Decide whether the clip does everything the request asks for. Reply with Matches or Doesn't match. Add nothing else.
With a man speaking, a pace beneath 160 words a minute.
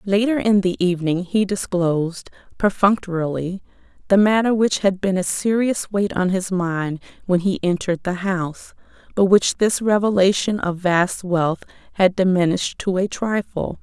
Doesn't match